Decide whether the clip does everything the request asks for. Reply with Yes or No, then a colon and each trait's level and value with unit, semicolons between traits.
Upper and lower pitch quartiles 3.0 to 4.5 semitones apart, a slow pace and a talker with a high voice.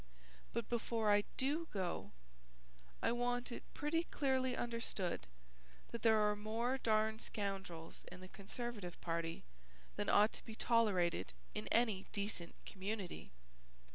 Yes: average, 3.9 semitones; slow, 130 wpm; high, 215 Hz